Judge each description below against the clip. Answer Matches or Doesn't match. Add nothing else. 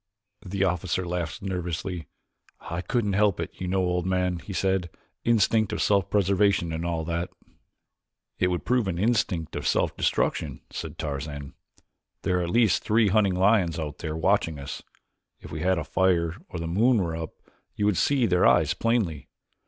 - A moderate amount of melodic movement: Matches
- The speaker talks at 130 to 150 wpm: Doesn't match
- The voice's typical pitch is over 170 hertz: Doesn't match